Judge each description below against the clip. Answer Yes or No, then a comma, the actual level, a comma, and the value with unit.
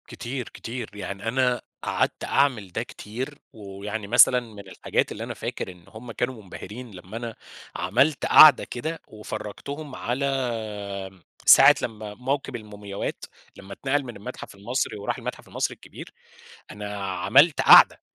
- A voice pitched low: Yes, low, 115 Hz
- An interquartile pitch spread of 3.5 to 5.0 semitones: Yes, average, 4.0 semitones